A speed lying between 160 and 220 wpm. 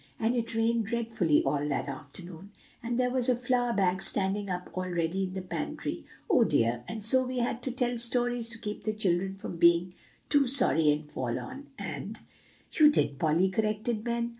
Yes: average, 190 wpm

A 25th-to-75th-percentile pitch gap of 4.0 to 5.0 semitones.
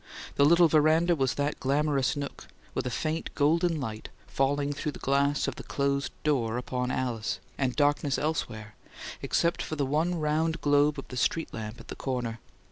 No: average, 3.2 semitones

